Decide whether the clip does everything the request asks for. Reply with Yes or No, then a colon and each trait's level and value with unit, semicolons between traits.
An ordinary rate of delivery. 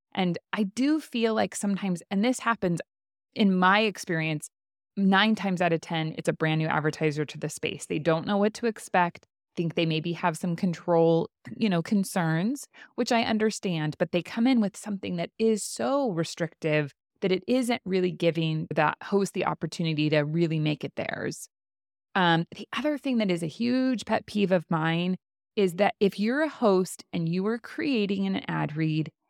Yes: average, 190 wpm